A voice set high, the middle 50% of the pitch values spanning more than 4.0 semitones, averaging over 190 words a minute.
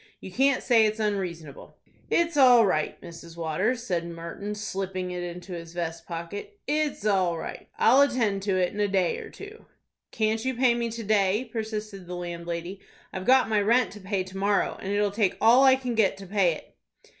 Yes: high, 200 Hz; average, 4.4 semitones; average, 200 wpm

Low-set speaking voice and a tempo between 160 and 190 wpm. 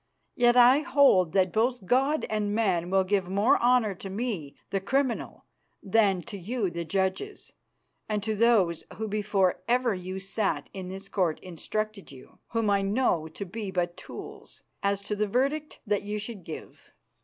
No: high, 205 Hz; average, 170 wpm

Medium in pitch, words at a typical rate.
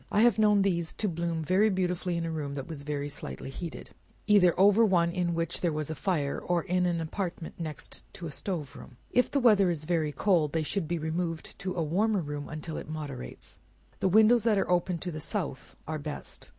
No: medium, 170 Hz; fast, 210 wpm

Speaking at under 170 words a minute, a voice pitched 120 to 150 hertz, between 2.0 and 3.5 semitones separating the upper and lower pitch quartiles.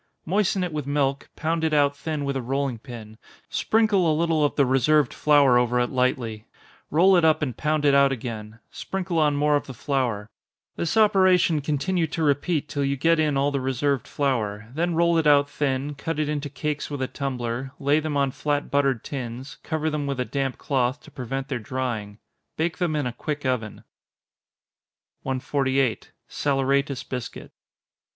No: average, 185 wpm; medium, 140 Hz; average, 2.9 semitones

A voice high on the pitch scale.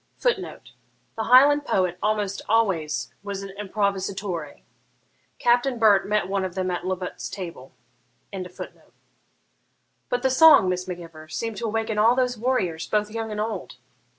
Yes: high, 205 Hz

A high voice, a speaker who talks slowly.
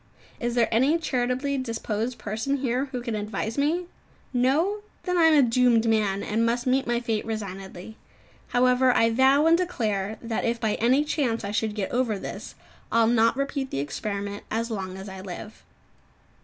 No: high, 235 Hz; average, 180 wpm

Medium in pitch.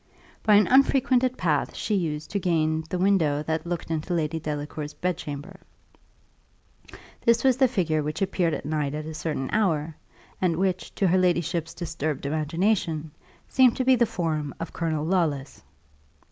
Yes: medium, 165 Hz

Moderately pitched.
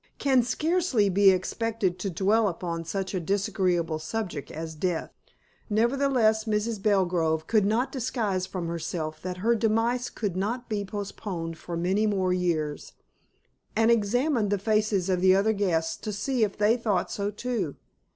No: high, 200 Hz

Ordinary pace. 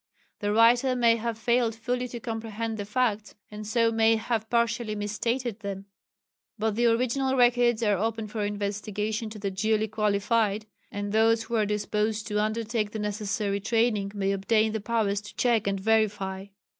Yes: average, 170 wpm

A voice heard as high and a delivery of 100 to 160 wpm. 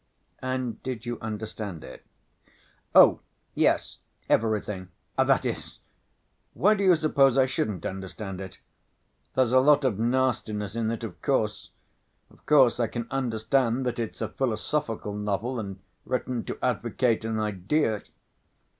No: low, 115 Hz; slow, 135 wpm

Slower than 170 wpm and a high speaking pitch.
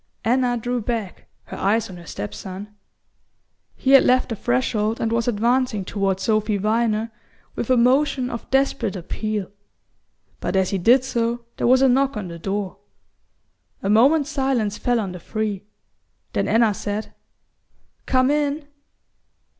Yes: average, 155 wpm; high, 225 Hz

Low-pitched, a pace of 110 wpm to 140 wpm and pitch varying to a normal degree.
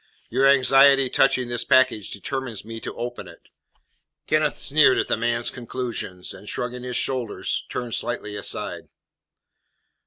No: low, 125 Hz; slow, 135 wpm; narrow, 2.3 semitones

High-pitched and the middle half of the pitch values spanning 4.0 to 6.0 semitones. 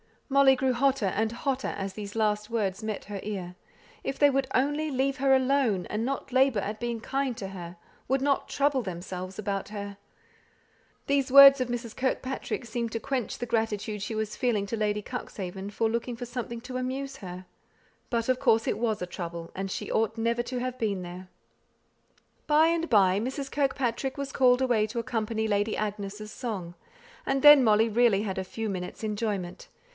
Yes: high, 230 Hz; average, 4.3 semitones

